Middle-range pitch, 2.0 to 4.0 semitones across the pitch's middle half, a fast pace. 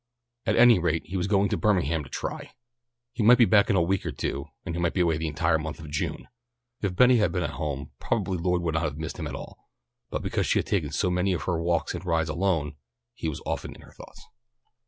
No: very low, 85 Hz; average, 3.3 semitones; fast, 260 wpm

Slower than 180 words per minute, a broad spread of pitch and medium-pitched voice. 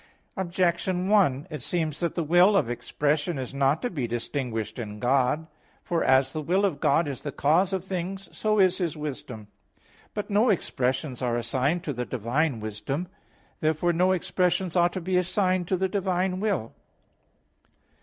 Yes: average, 170 wpm; wide, 5.8 semitones; medium, 165 Hz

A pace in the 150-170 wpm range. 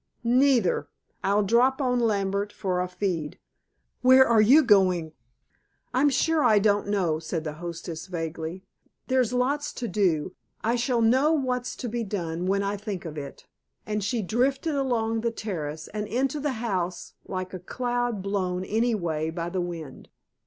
Yes: average, 165 wpm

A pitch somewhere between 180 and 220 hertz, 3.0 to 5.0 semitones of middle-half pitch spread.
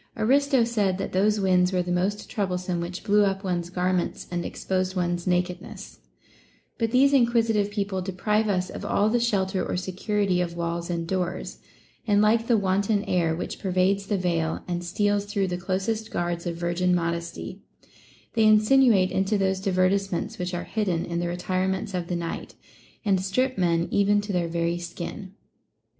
No: high, 190 Hz; narrow, 2.6 semitones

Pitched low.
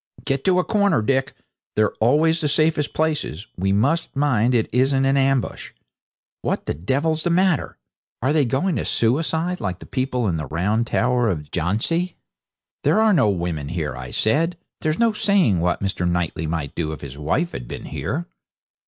Yes: low, 130 Hz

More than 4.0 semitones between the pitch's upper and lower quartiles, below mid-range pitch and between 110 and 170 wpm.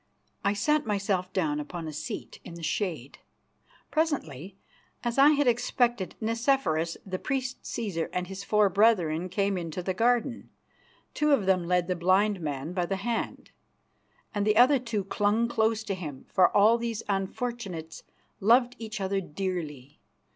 No: average, 4.9 semitones; high, 195 Hz; average, 155 wpm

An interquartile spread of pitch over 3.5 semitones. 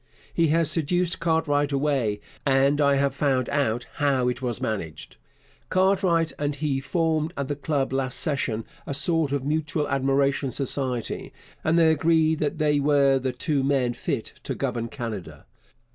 No: average, 2.8 semitones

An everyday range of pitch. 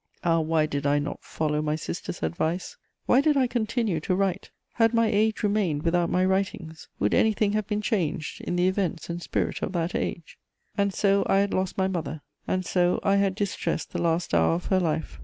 Yes: average, 3.9 semitones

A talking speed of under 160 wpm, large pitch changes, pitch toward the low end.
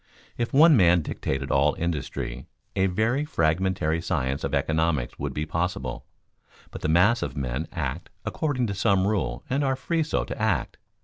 No: average, 170 wpm; wide, 7.4 semitones; very low, 90 Hz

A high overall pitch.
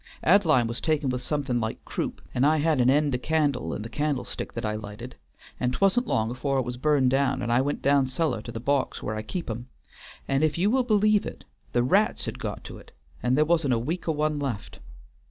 No: low, 135 Hz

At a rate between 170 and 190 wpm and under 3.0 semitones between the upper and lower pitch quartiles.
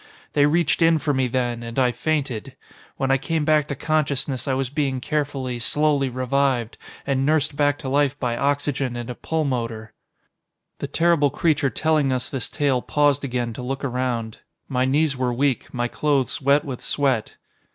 Yes: average, 175 wpm; narrow, 2.6 semitones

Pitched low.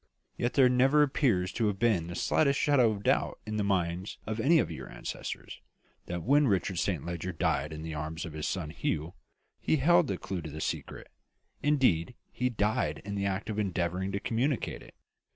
Yes: low, 100 Hz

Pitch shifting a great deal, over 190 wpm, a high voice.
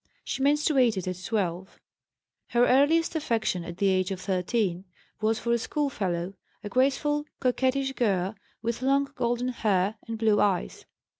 No: wide, 5.7 semitones; average, 145 wpm; high, 225 Hz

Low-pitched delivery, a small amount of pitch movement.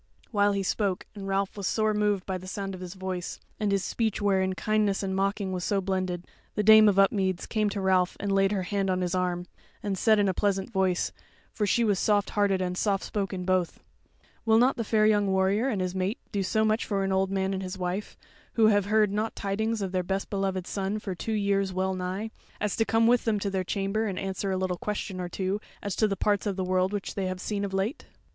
No: high, 195 Hz; narrow, 1.9 semitones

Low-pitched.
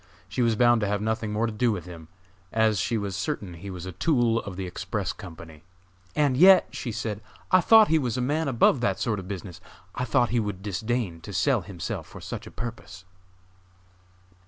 Yes: low, 110 Hz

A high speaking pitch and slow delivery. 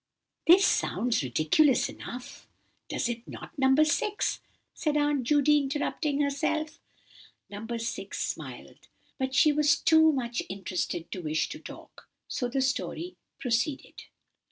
Yes: very high, 270 Hz; slow, 130 wpm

